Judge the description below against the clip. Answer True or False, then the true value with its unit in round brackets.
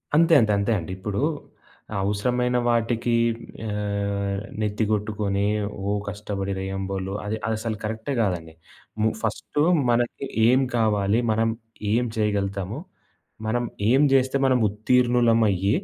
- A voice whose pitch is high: False (105 Hz)